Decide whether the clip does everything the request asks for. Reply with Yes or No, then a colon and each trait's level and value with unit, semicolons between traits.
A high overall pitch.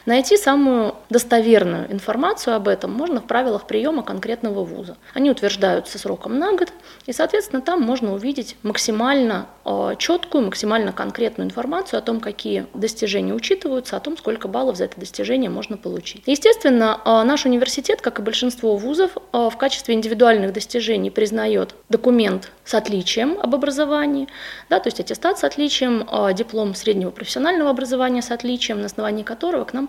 Yes: high, 240 Hz